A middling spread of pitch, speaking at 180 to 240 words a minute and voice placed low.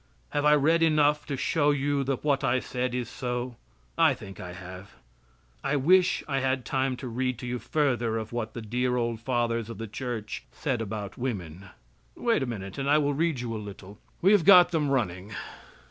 Yes: average, 4.4 semitones; average, 200 wpm; low, 125 Hz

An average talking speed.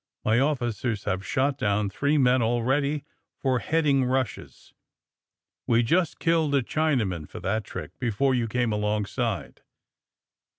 No: slow, 130 wpm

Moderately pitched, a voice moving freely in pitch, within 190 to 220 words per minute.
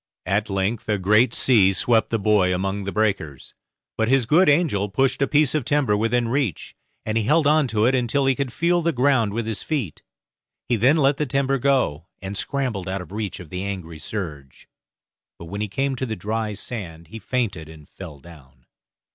No: low, 110 Hz; wide, 5.7 semitones; fast, 205 wpm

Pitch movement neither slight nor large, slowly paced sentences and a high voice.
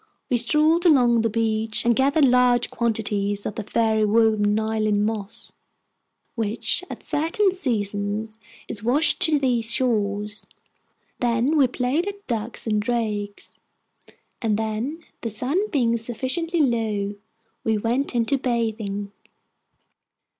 Yes: average, 3.4 semitones; slow, 125 wpm; high, 230 Hz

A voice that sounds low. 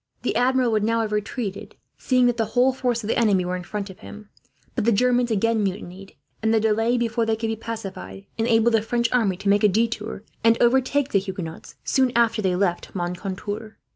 No: high, 220 Hz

